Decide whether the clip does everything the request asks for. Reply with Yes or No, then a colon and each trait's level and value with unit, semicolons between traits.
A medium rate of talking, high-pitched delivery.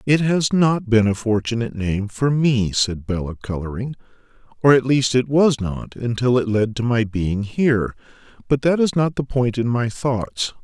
No: average, 180 wpm; low, 120 Hz